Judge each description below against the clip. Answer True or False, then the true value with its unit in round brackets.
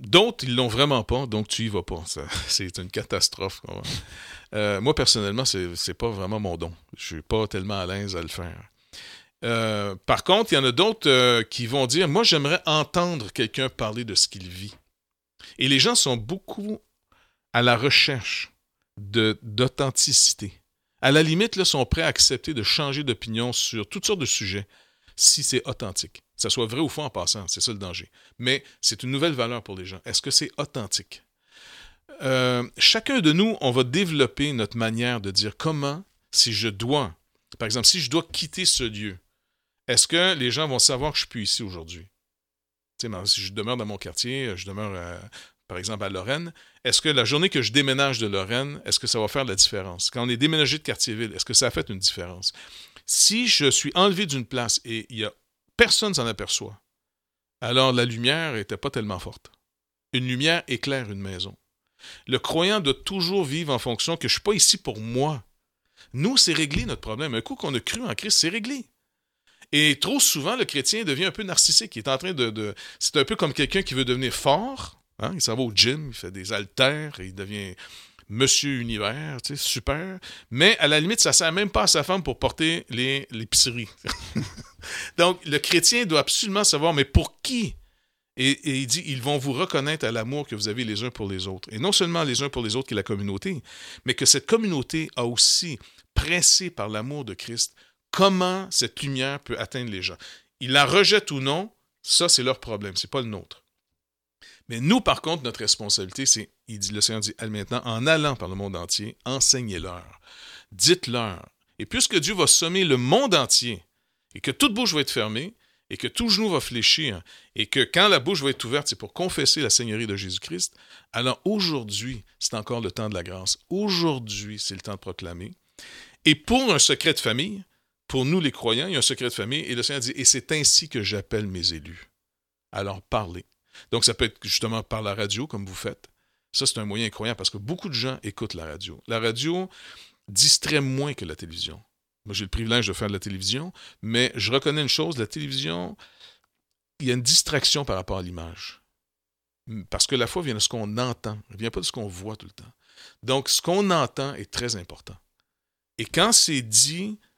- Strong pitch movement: True (6.4 semitones)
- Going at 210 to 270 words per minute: True (215 wpm)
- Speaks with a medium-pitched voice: False (120 Hz)